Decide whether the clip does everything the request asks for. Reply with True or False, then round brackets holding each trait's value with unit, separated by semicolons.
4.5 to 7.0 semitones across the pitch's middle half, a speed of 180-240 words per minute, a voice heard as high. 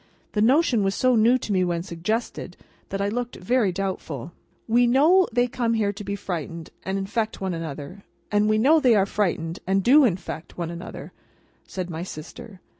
True (5.0 semitones; 190 wpm; 200 Hz)